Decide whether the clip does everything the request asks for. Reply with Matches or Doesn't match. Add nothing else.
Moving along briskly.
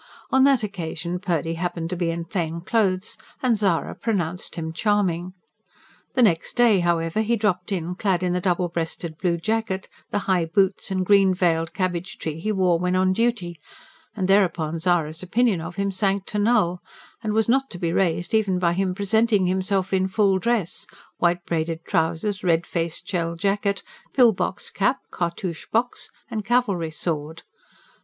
Doesn't match